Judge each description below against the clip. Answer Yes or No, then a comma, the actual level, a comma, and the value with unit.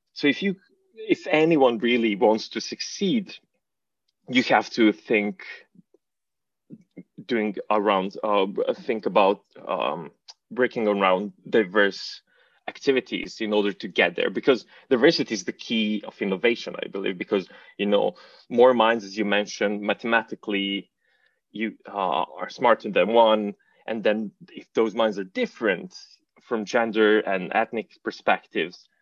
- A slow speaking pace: Yes, slow, 130 wpm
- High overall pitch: No, low, 110 Hz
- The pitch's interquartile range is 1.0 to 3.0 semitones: No, average, 3.4 semitones